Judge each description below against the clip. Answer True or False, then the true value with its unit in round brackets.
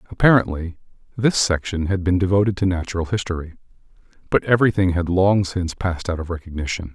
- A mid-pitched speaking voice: False (90 Hz)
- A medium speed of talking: True (155 wpm)